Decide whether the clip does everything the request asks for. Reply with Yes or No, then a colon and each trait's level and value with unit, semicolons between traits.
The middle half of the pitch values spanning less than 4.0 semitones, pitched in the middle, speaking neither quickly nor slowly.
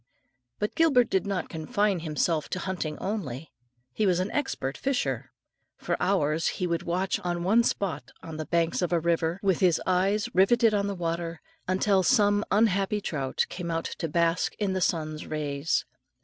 Yes: average, 3.5 semitones; medium, 180 Hz; average, 175 wpm